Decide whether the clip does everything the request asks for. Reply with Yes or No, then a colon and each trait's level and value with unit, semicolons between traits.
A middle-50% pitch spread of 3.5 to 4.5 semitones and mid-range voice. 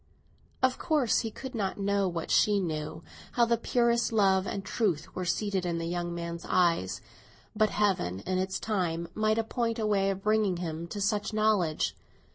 No: average, 3.9 semitones; high, 195 Hz